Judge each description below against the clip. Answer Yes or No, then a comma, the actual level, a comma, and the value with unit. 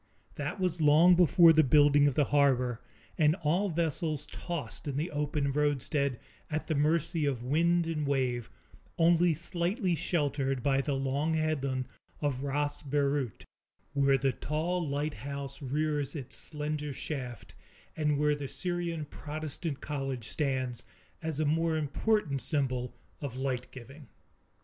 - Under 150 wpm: Yes, average, 140 wpm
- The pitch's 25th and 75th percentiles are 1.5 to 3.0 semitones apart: Yes, average, 2.7 semitones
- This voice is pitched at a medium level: Yes, medium, 145 Hz